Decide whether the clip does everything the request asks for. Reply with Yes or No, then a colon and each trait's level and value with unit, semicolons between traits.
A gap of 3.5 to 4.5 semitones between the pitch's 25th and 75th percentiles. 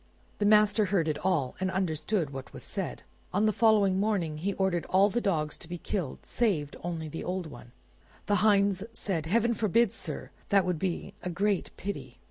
Yes: average, 3.9 semitones